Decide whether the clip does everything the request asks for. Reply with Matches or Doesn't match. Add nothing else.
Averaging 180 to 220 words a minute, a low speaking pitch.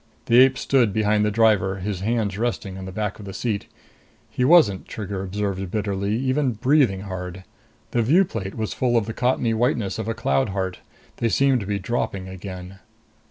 Matches